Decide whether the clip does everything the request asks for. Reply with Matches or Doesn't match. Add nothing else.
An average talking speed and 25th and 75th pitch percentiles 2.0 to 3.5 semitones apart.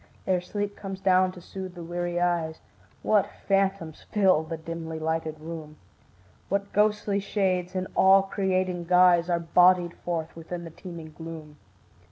Matches